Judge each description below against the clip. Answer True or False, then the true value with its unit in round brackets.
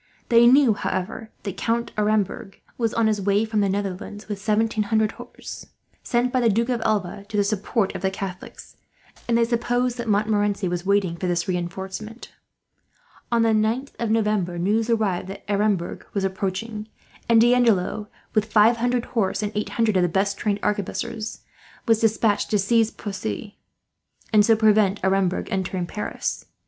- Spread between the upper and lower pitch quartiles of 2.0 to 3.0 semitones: True (2.6 semitones)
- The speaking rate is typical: True (170 wpm)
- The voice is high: True (210 Hz)